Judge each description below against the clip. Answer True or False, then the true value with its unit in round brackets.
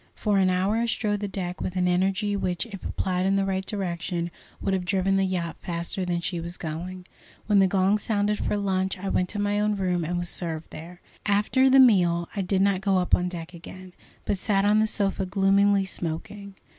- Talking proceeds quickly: True (220 wpm)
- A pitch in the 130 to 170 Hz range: False (190 Hz)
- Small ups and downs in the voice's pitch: True (2.1 semitones)